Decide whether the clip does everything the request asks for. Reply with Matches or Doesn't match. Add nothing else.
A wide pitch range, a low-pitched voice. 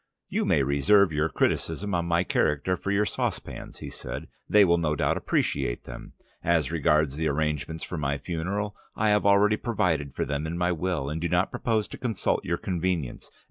Doesn't match